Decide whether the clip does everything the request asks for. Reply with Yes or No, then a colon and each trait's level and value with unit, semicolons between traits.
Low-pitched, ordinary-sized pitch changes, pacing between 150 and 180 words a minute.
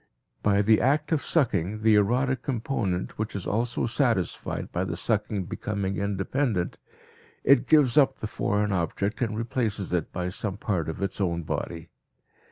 Yes: low, 105 Hz; average, 4.2 semitones; average, 160 wpm